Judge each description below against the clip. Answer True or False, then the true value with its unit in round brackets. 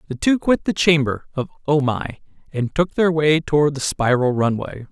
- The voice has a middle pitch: True (145 Hz)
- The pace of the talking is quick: False (195 wpm)